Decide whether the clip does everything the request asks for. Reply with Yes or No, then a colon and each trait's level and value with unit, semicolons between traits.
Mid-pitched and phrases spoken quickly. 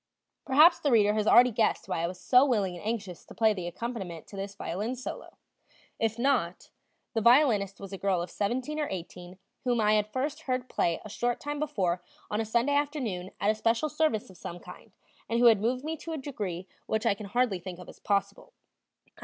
No: high, 220 Hz; fast, 220 wpm